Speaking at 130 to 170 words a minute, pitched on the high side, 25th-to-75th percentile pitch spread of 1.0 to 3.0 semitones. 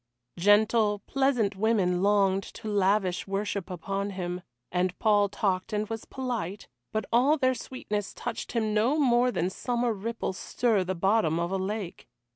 No: average, 155 wpm; high, 205 Hz; average, 3.4 semitones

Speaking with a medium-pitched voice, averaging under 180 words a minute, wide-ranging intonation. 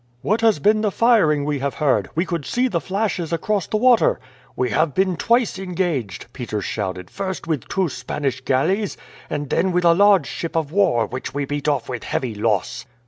No: medium, 165 Hz; average, 195 wpm; wide, 7.0 semitones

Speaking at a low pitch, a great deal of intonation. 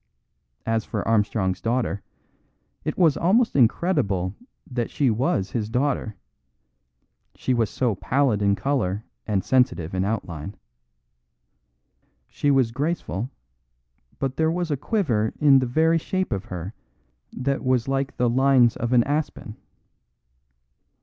No: low, 125 Hz; average, 4.8 semitones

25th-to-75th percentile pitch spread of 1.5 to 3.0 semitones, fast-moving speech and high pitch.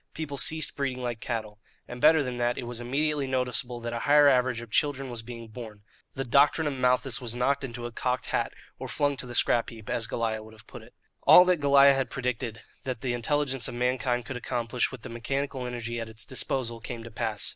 No: narrow, 2.6 semitones; fast, 225 wpm; low, 125 Hz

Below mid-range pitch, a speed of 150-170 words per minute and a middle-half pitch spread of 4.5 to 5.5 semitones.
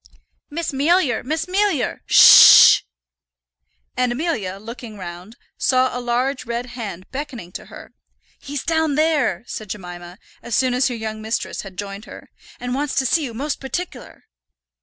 No: high, 245 Hz; average, 160 wpm; average, 5.1 semitones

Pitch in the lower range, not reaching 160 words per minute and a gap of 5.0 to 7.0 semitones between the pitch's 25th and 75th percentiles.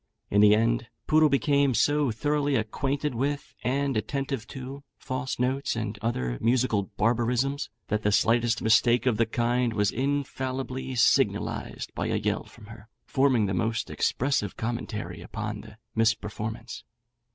No: low, 120 Hz; average, 140 wpm; average, 3.6 semitones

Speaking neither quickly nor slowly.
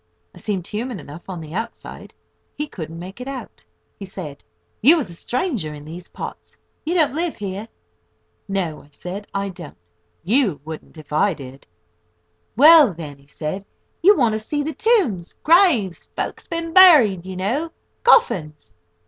Yes: average, 155 wpm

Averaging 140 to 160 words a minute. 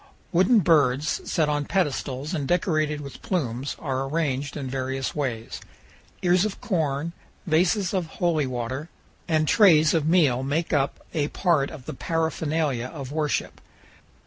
Yes: average, 145 wpm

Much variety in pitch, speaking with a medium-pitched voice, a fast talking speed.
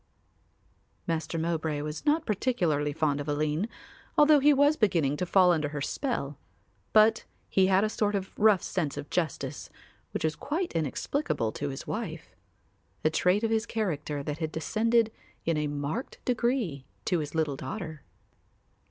No: wide, 6.7 semitones; medium, 170 Hz; average, 160 wpm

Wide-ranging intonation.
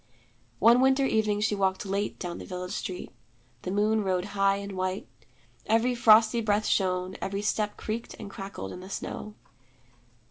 No: narrow, 2.5 semitones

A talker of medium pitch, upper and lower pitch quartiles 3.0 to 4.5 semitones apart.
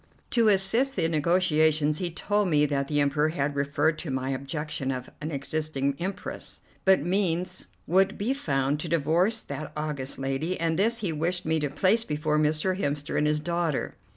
Yes: medium, 155 Hz; average, 4.0 semitones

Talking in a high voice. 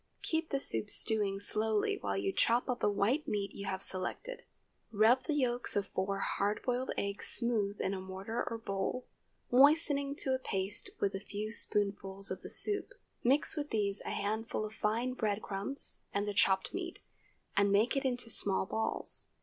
Yes: high, 215 Hz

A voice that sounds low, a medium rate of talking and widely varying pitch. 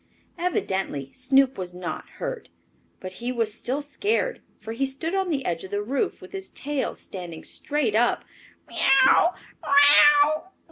No: very high, 260 Hz; average, 145 wpm; wide, 6.5 semitones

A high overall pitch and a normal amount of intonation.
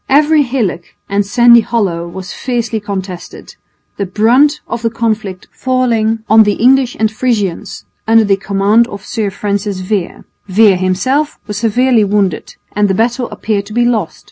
Yes: high, 215 Hz; average, 3.2 semitones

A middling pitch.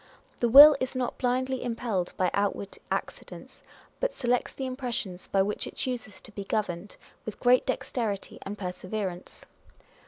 No: high, 225 Hz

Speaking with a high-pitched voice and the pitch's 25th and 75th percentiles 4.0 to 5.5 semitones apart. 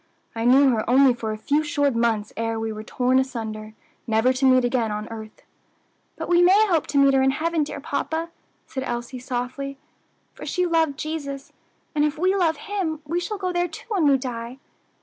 Yes: very high, 270 Hz; average, 5.1 semitones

